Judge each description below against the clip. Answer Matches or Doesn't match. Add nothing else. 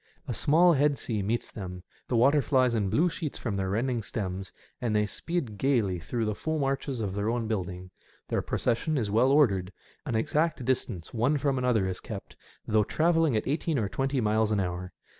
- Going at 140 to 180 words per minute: Doesn't match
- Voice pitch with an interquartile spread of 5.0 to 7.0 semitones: Matches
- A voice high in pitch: Doesn't match